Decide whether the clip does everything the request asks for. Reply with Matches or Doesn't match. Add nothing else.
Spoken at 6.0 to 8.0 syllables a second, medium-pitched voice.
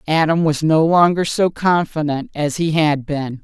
Doesn't match